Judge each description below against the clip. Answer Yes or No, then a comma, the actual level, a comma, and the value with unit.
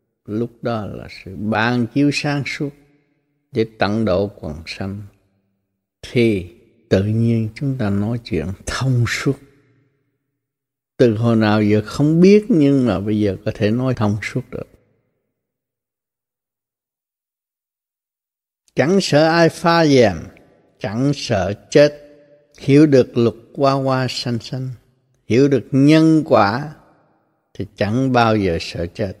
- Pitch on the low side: Yes, low, 120 Hz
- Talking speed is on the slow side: Yes, slow, 130 wpm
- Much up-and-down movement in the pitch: No, average, 5.0 semitones